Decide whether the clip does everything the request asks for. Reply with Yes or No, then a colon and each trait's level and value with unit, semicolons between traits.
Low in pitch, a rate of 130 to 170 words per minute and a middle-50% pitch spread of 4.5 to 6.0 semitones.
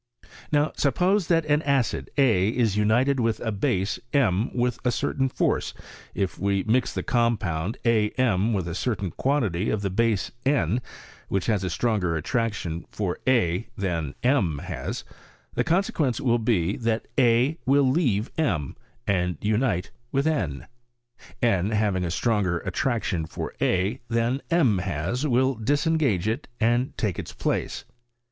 Yes: low, 115 Hz; average, 155 wpm; average, 5.2 semitones